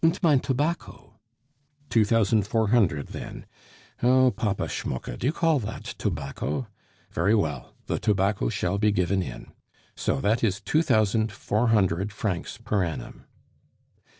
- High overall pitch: No, low, 105 Hz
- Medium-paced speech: Yes, average, 145 wpm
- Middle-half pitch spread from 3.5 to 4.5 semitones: Yes, average, 3.9 semitones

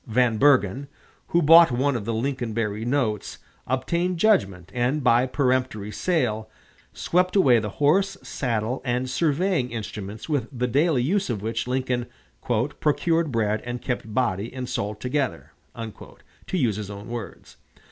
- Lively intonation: No, average, 4.5 semitones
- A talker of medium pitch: No, low, 125 Hz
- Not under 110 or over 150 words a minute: Yes, average, 145 wpm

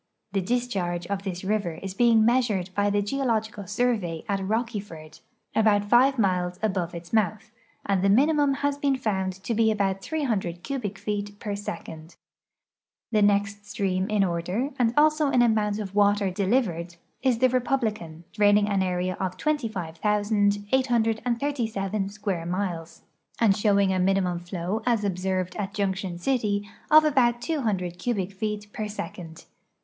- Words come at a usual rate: Yes, average, 150 wpm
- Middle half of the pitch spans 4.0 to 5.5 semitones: No, average, 3.6 semitones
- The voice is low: No, high, 205 Hz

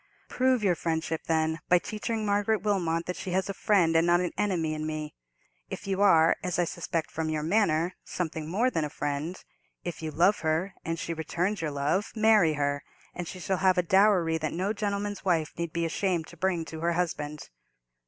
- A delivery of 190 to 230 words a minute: Yes, average, 200 wpm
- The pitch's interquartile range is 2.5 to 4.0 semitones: Yes, average, 3.4 semitones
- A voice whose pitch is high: No, medium, 170 Hz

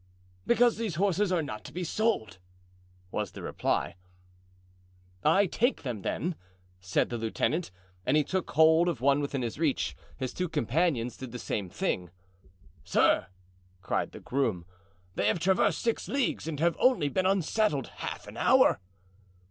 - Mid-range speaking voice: Yes, medium, 155 Hz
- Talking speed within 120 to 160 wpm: Yes, average, 155 wpm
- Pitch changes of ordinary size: No, wide, 7.2 semitones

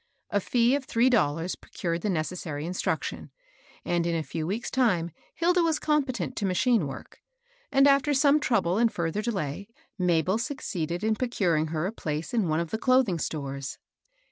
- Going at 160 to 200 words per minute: Yes, average, 180 wpm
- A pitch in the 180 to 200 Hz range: Yes, high, 190 Hz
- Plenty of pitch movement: Yes, wide, 7.1 semitones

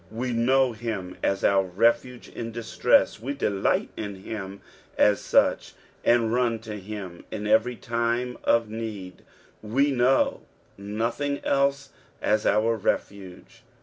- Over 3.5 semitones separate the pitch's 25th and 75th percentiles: No, average, 3.0 semitones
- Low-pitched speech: Yes, low, 115 Hz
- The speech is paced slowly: Yes, slow, 130 wpm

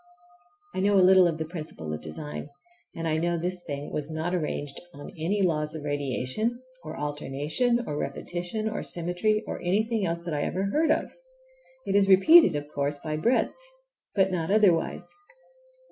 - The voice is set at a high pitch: No, medium, 170 Hz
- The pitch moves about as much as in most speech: Yes, average, 4.8 semitones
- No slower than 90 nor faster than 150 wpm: No, average, 175 wpm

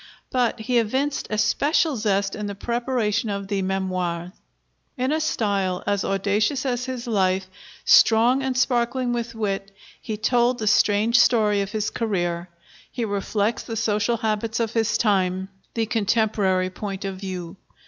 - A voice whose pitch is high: Yes, high, 215 Hz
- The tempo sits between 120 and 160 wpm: Yes, average, 150 wpm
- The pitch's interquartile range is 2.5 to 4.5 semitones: Yes, average, 3.4 semitones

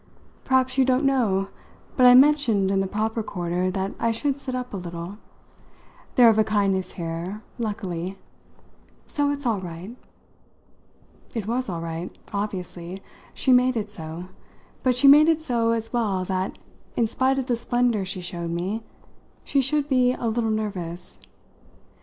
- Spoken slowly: No, average, 160 wpm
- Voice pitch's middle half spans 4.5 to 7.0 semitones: Yes, average, 5.2 semitones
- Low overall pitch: No, high, 215 Hz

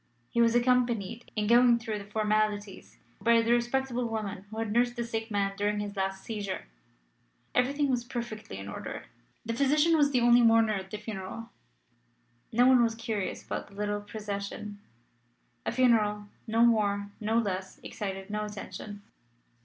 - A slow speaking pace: No, average, 160 wpm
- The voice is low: No, high, 220 Hz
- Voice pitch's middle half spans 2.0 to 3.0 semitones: Yes, narrow, 2.5 semitones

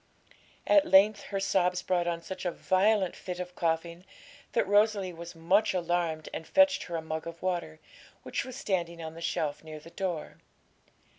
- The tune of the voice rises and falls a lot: No, narrow, 2.6 semitones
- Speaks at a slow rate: No, average, 175 wpm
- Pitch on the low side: No, medium, 175 Hz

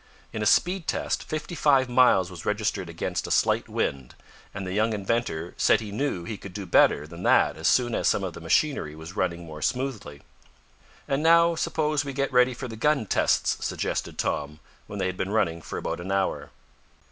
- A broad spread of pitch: Yes, wide, 7.3 semitones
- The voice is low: Yes, low, 105 Hz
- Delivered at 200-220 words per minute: Yes, fast, 205 wpm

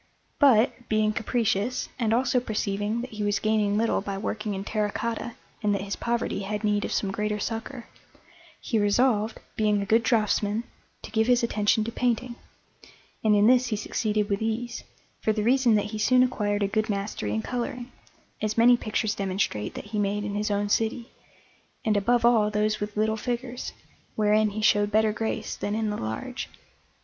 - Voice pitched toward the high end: Yes, high, 215 Hz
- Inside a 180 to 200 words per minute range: Yes, average, 185 wpm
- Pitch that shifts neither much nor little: No, narrow, 2.0 semitones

